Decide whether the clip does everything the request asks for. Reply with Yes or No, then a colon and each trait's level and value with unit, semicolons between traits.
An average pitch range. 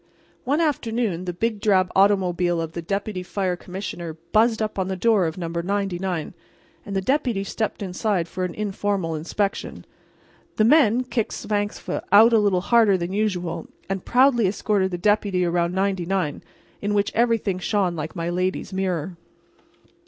Yes: average, 3.0 semitones